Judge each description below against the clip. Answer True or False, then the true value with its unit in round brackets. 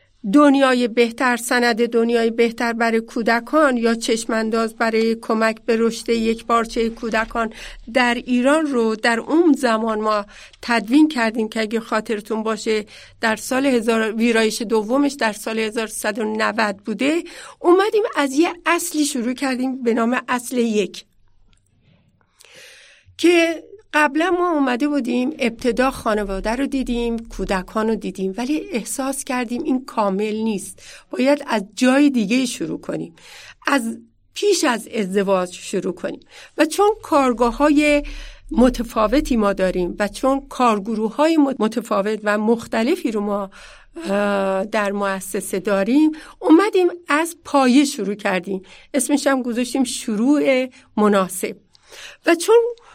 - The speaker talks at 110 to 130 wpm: True (125 wpm)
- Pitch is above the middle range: True (235 Hz)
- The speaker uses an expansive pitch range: False (4.2 semitones)